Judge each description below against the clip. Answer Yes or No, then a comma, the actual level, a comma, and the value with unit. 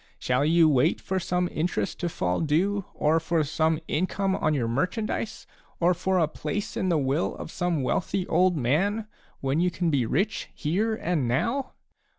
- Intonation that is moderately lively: Yes, average, 3.9 semitones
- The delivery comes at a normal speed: Yes, average, 175 wpm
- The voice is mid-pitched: Yes, medium, 170 Hz